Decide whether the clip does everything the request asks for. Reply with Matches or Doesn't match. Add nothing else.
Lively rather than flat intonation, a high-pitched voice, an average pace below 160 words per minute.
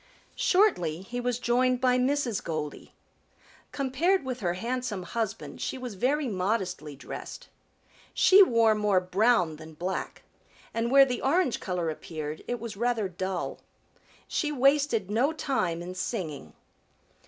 Matches